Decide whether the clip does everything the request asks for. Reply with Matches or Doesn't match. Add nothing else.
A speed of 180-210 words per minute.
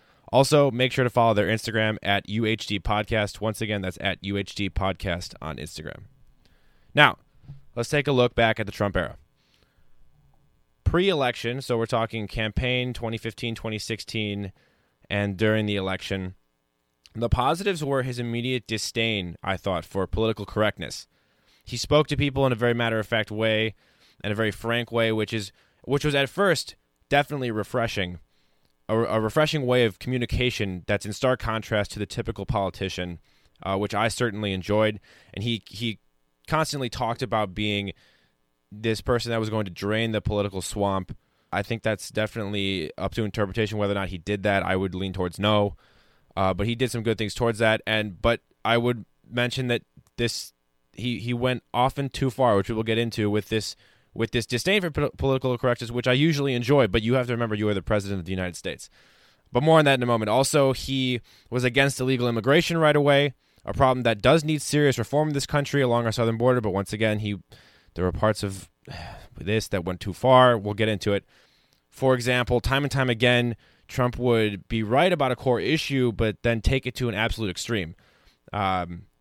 Matches